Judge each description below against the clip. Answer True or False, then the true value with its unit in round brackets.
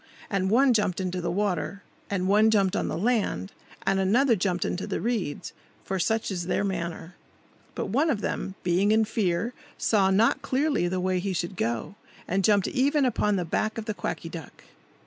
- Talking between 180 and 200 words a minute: True (190 wpm)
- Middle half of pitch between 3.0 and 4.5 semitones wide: True (3.5 semitones)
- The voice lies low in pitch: False (195 Hz)